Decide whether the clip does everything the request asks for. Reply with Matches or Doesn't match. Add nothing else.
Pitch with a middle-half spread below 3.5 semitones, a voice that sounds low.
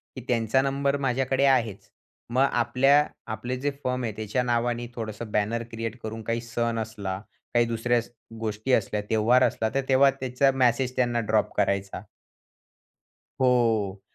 Matches